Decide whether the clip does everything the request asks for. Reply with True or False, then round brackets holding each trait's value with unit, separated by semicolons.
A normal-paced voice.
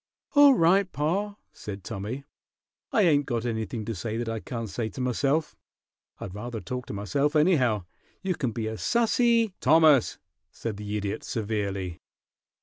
True (160 wpm)